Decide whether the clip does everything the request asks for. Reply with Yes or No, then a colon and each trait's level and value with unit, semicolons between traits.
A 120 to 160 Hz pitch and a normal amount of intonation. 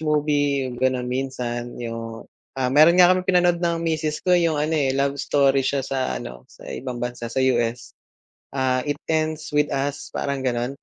Yes: medium, 140 Hz; average, 3.6 semitones